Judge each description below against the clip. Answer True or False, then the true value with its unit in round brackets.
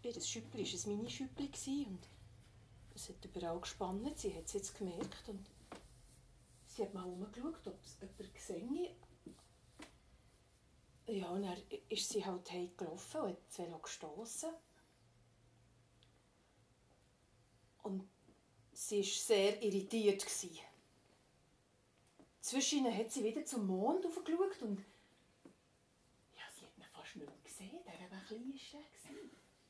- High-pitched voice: True (200 Hz)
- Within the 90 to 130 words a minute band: True (125 wpm)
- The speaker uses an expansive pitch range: True (6.9 semitones)